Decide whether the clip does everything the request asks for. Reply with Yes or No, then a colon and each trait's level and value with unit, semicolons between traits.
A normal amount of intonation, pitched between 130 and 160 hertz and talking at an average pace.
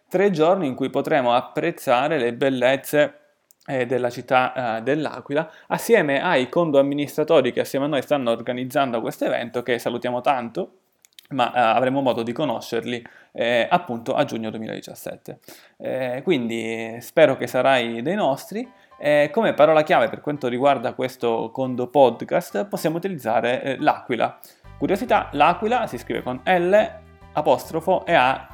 Yes: average, 4.5 semitones; low, 135 Hz; average, 145 wpm